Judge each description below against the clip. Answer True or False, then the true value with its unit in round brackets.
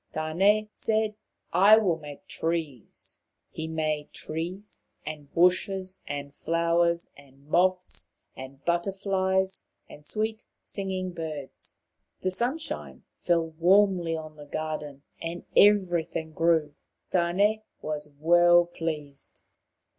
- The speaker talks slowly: True (110 wpm)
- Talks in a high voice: False (170 Hz)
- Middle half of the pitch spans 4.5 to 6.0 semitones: False (3.4 semitones)